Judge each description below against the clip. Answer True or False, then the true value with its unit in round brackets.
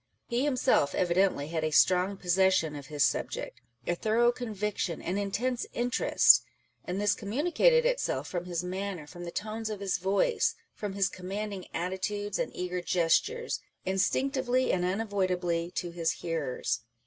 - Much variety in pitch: False (3.9 semitones)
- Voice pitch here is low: False (190 Hz)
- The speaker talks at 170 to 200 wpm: False (150 wpm)